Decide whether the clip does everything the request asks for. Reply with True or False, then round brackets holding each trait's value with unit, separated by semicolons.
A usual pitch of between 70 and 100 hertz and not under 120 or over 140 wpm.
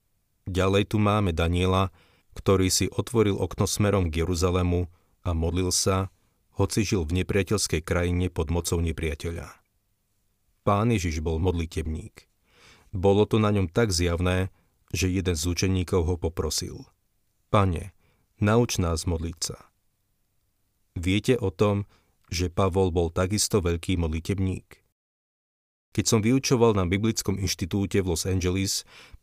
True (95 Hz; 125 wpm)